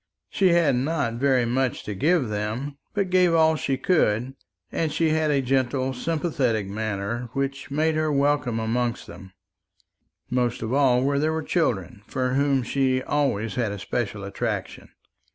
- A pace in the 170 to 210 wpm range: No, average, 160 wpm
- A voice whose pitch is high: No, low, 130 Hz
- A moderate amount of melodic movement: Yes, average, 4.2 semitones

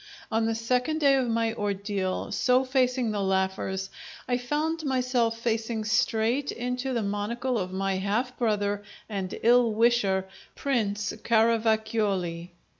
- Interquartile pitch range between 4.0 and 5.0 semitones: No, average, 3.5 semitones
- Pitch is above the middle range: Yes, high, 225 Hz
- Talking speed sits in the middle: No, slow, 130 wpm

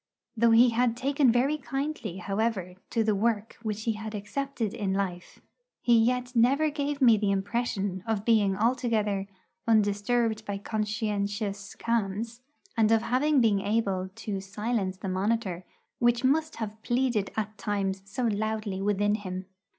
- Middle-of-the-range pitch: No, high, 220 Hz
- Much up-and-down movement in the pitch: No, average, 3.0 semitones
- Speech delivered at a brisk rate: No, average, 150 wpm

